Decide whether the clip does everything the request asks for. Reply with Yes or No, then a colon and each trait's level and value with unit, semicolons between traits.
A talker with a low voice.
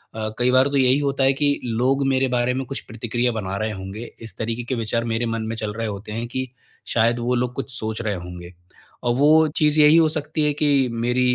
Yes: low, 120 Hz